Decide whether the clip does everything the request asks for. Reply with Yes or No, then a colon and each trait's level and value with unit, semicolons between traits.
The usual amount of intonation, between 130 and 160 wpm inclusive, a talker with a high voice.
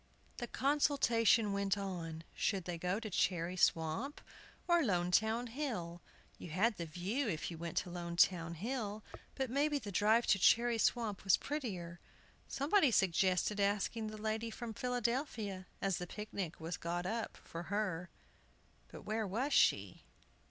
Yes: average, 4.9 semitones; average, 150 wpm; high, 205 Hz